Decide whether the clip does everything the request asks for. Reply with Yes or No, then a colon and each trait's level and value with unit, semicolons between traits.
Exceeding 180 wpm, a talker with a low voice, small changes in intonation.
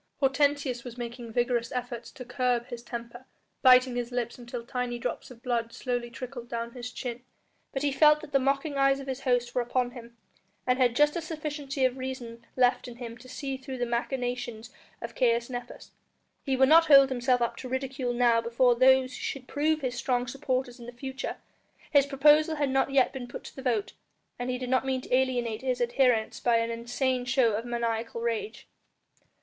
No: average, 200 wpm; very high, 250 Hz; narrow, 1.9 semitones